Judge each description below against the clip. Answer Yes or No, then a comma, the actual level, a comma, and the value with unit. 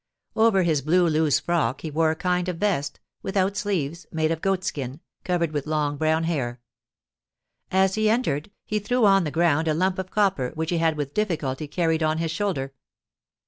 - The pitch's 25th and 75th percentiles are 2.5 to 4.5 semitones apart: Yes, average, 3.8 semitones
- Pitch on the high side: No, medium, 165 Hz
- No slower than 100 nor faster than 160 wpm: No, average, 185 wpm